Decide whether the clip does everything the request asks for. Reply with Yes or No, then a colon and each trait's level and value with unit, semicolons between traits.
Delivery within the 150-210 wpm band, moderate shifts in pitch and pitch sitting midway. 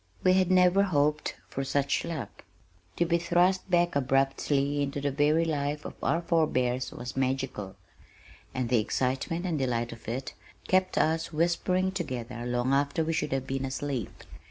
Yes: average, 160 wpm; average, 4.4 semitones; medium, 145 Hz